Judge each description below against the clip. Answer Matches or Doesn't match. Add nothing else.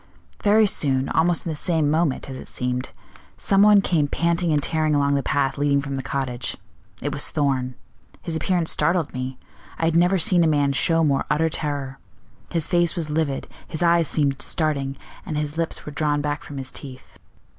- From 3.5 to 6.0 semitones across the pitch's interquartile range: Doesn't match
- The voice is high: Doesn't match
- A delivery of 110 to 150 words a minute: Doesn't match